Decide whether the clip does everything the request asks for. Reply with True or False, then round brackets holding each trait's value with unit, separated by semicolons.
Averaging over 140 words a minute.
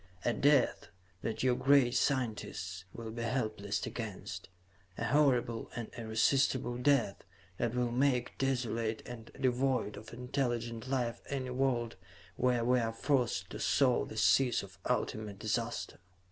False (135 wpm)